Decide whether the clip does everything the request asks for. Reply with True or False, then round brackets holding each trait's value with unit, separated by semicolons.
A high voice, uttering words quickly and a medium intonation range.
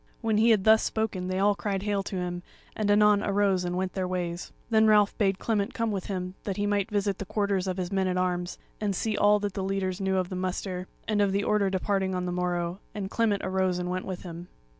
False (195 Hz; 250 wpm; 2.0 semitones)